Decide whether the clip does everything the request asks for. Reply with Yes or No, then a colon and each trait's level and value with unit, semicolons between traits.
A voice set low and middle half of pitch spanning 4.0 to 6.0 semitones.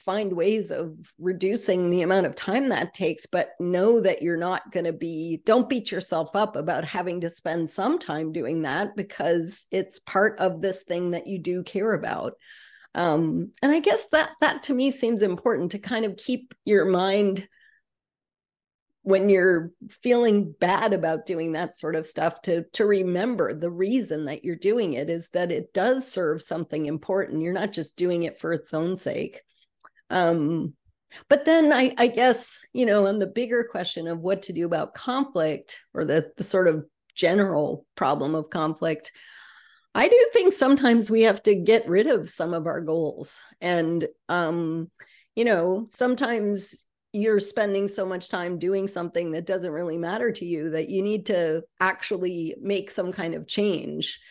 No: medium, 185 Hz; average, 4.4 semitones